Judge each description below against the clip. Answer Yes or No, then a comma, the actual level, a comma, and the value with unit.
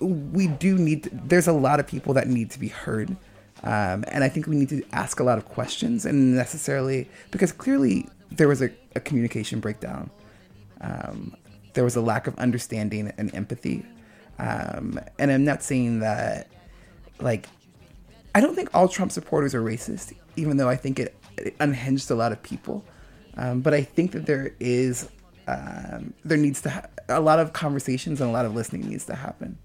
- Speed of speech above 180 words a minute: Yes, average, 190 wpm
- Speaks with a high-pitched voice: No, low, 135 Hz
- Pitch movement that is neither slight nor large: Yes, average, 4.7 semitones